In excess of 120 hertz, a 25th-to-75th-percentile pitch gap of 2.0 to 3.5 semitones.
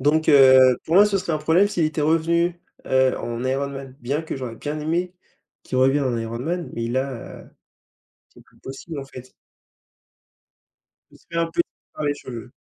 No: medium, 140 Hz; average, 4.0 semitones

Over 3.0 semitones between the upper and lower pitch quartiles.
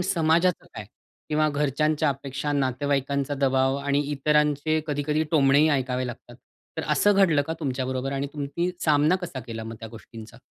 No: narrow, 2.6 semitones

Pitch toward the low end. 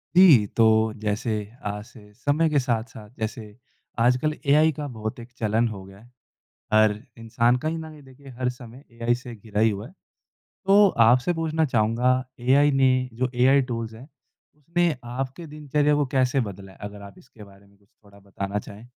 Yes: low, 120 Hz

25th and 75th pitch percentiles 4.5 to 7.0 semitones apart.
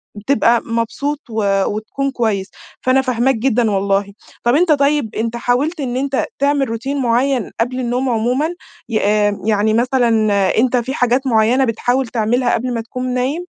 No: average, 2.9 semitones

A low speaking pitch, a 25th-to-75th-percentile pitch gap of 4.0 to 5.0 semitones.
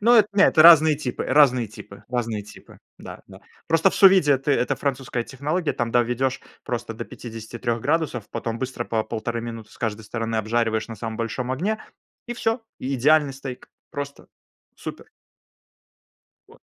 Yes: low, 125 Hz; average, 4.6 semitones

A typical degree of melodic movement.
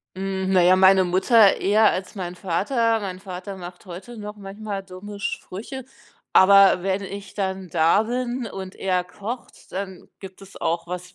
No: narrow, 2.0 semitones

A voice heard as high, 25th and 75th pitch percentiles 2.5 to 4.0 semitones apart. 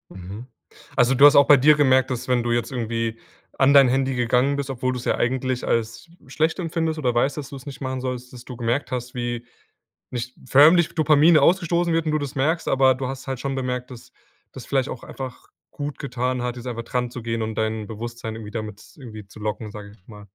No: low, 125 Hz; average, 2.9 semitones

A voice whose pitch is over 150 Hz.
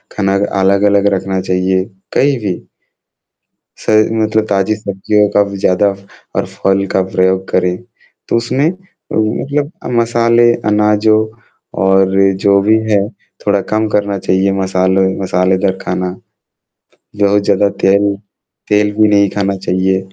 No: low, 100 Hz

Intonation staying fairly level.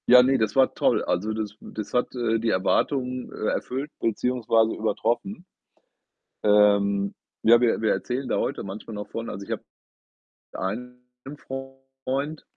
No: average, 3.6 semitones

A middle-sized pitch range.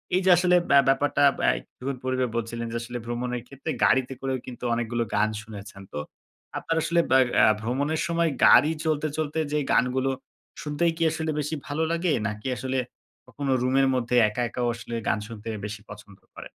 Yes: average, 4.3 semitones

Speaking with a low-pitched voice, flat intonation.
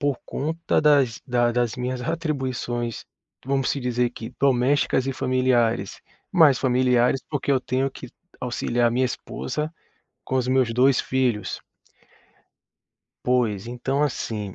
Yes: low, 125 Hz; narrow, 2.0 semitones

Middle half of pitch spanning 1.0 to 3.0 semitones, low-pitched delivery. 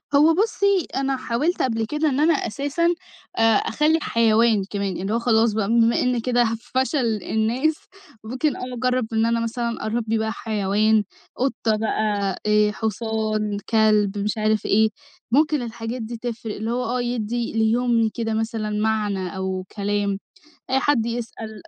No: narrow, 2.5 semitones; high, 225 Hz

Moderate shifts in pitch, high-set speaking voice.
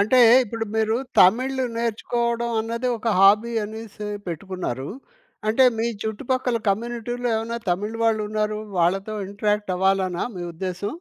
Yes: average, 3.2 semitones; high, 215 Hz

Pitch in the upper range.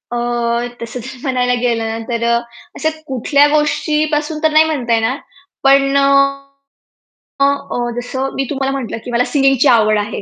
Yes: very high, 265 Hz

